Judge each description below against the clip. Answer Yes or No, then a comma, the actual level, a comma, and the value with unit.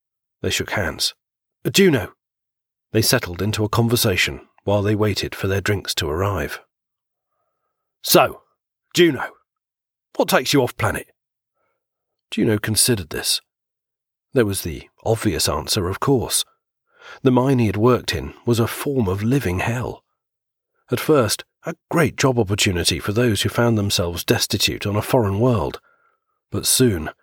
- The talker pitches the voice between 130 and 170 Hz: No, low, 115 Hz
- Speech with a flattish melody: No, average, 3.8 semitones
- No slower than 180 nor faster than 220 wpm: No, average, 145 wpm